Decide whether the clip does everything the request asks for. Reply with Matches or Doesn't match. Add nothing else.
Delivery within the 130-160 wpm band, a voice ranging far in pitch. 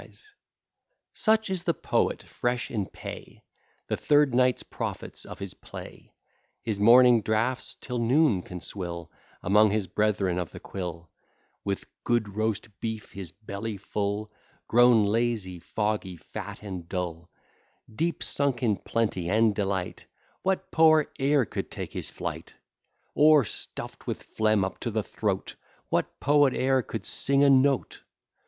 Doesn't match